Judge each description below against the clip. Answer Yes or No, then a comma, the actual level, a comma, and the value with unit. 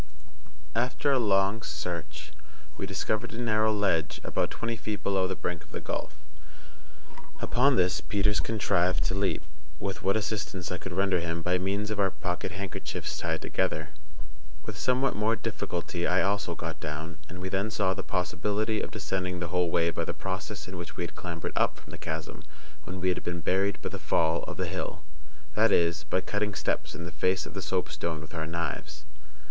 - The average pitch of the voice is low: Yes, very low, 95 Hz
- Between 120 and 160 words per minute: No, average, 190 wpm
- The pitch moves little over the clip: No, average, 3.3 semitones